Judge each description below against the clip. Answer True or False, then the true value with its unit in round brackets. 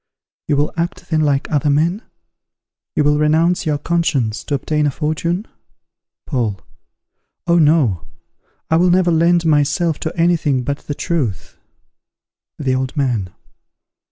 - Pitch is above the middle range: False (150 Hz)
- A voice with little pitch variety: False (3.3 semitones)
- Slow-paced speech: False (145 wpm)